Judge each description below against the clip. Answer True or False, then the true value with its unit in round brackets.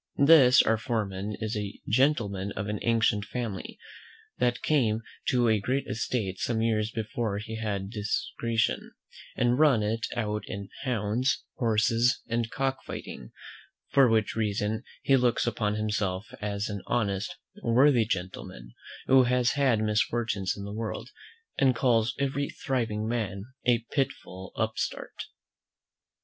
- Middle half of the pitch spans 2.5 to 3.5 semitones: True (2.8 semitones)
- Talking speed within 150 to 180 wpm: False (135 wpm)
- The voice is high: False (110 Hz)